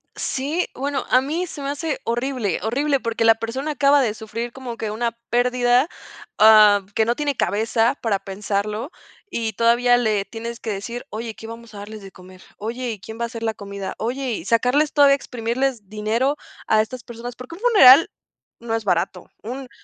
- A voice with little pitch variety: No, average, 3.2 semitones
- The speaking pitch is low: No, high, 235 Hz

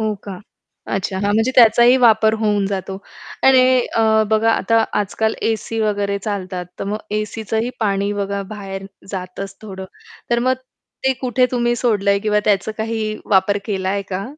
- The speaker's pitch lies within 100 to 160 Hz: No, high, 210 Hz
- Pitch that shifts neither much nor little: No, narrow, 2.2 semitones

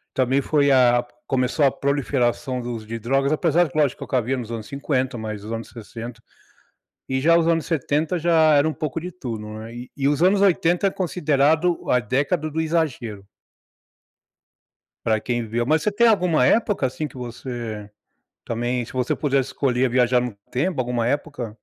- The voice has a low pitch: Yes, low, 130 Hz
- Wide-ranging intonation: No, average, 4.6 semitones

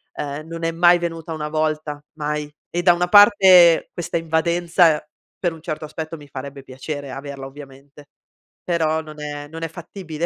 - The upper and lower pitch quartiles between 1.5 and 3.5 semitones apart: Yes, narrow, 2.5 semitones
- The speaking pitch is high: No, medium, 155 Hz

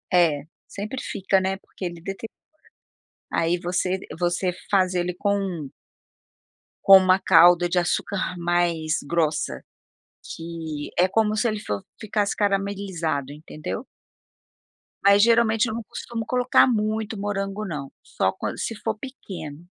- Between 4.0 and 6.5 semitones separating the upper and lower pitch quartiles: No, average, 3.5 semitones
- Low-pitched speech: No, high, 190 Hz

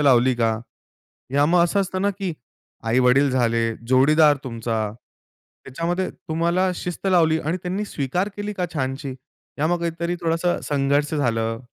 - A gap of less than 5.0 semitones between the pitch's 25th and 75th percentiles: No, wide, 5.4 semitones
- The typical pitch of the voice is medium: Yes, medium, 155 Hz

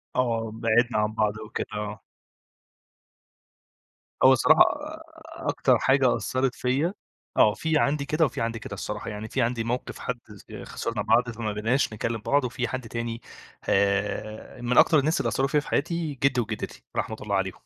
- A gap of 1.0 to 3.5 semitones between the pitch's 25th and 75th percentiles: No, average, 4.3 semitones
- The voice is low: Yes, low, 120 Hz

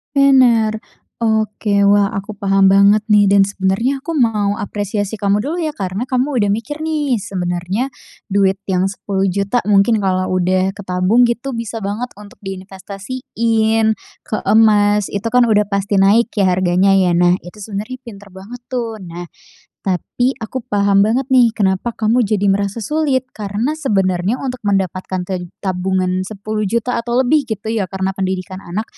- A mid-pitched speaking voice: No, high, 205 Hz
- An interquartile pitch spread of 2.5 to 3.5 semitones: Yes, average, 3.2 semitones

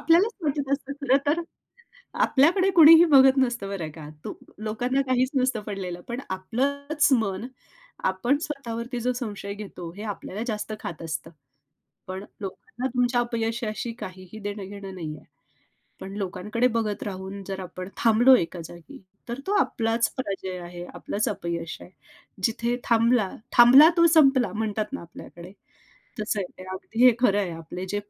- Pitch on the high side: Yes, high, 220 Hz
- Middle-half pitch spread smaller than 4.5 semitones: No, average, 5.2 semitones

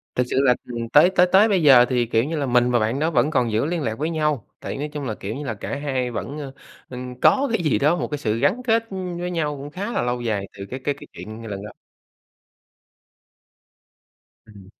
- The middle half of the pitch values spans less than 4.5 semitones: No, average, 4.9 semitones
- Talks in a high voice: No, low, 135 Hz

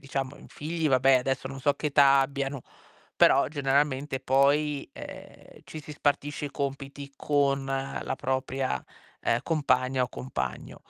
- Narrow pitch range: Yes, narrow, 1.3 semitones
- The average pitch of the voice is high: No, medium, 140 Hz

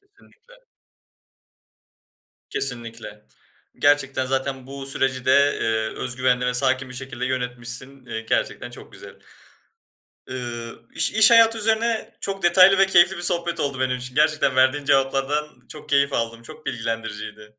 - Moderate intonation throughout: Yes, average, 3.7 semitones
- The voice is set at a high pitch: No, low, 135 Hz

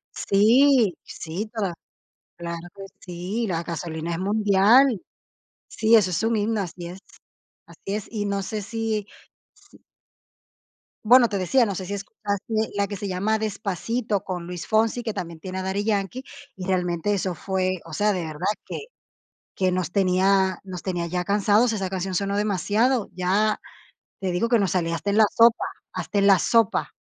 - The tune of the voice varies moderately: Yes, average, 3.0 semitones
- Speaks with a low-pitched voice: No, high, 195 Hz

